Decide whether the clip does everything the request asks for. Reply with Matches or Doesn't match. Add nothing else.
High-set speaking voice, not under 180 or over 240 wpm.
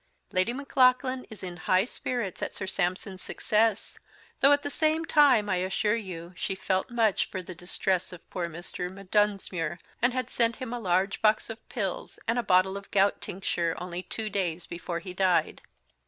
Matches